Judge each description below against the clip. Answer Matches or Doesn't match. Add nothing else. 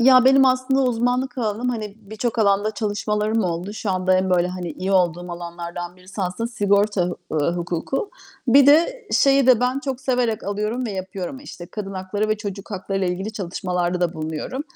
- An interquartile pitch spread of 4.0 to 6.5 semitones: Matches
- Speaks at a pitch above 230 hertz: Doesn't match